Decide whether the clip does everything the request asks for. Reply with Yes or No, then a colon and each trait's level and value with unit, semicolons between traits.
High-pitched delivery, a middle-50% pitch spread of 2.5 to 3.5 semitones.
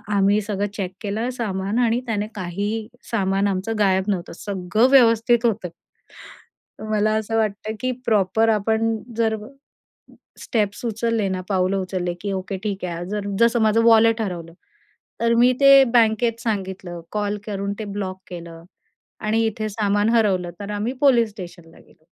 Yes: high, 210 Hz; average, 2.8 semitones